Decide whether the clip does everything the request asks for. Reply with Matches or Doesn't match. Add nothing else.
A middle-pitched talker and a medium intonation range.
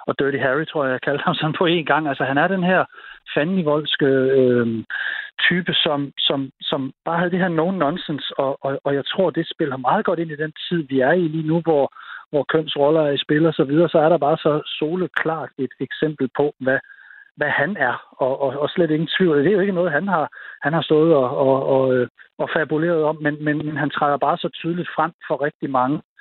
Matches